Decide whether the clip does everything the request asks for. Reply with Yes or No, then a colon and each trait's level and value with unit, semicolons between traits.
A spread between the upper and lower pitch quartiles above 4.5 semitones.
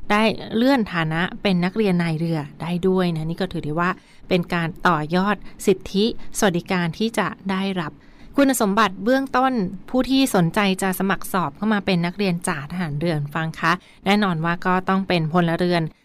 No: average, 3.3 semitones